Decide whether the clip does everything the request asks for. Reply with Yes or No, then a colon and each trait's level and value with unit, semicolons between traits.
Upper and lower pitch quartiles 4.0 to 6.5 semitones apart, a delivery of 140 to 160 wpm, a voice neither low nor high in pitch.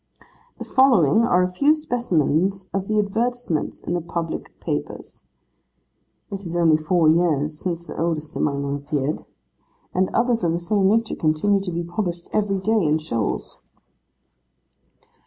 Yes: average, 4.6 semitones; average, 150 wpm; medium, 175 Hz